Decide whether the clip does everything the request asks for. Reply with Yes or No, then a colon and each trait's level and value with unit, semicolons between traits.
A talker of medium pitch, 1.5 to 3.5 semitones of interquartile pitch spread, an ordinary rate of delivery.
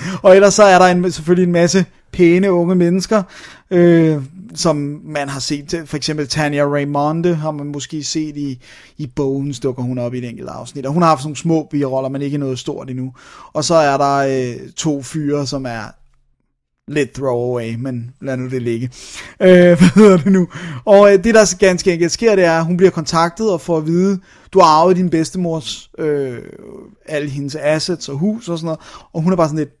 No: medium, 155 Hz; average, 4.2 semitones; average, 215 wpm